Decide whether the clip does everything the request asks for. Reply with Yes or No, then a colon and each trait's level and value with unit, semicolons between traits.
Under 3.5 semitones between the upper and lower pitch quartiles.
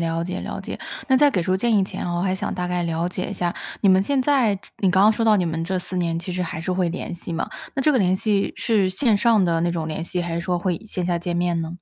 Yes: average, 2.8 semitones